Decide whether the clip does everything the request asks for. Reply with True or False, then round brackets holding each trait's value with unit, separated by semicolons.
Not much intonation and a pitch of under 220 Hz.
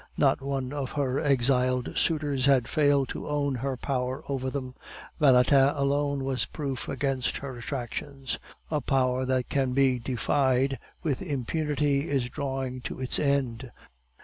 True (1.7 semitones; 135 Hz)